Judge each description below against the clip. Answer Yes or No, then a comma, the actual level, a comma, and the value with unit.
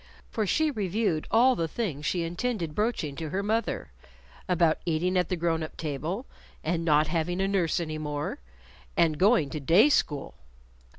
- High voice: No, medium, 170 Hz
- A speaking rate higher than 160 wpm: Yes, average, 170 wpm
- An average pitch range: Yes, average, 4.4 semitones